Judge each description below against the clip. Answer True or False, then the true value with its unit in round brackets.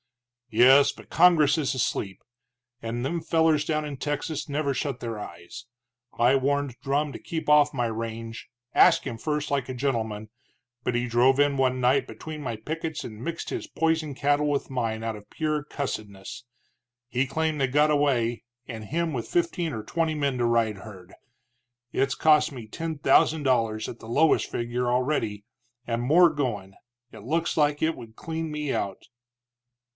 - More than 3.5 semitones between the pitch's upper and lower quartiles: True (4.6 semitones)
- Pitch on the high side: False (135 Hz)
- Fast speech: False (170 wpm)